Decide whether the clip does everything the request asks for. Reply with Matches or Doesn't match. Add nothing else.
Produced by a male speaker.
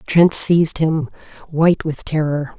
Doesn't match